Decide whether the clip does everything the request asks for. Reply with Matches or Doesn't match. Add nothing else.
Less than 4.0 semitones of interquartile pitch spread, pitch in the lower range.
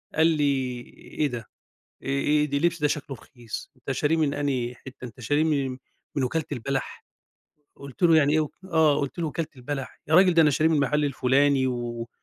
Doesn't match